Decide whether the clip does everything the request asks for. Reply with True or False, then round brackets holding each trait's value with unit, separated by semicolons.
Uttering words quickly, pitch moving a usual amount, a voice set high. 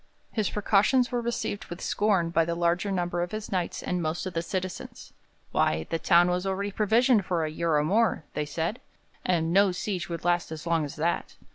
False (210 wpm; 3.2 semitones; 175 Hz)